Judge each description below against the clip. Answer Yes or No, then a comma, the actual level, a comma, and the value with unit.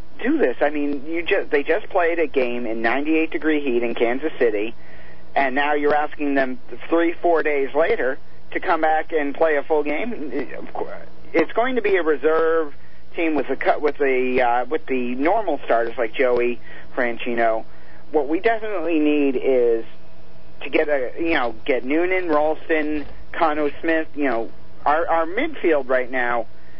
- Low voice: No, medium, 150 Hz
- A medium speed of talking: Yes, average, 170 wpm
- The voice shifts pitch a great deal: No, average, 4.1 semitones